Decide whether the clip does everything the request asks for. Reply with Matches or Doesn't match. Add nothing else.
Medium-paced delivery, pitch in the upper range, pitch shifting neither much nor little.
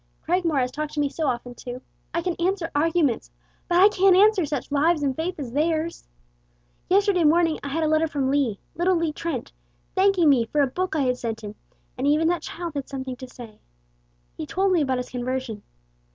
Doesn't match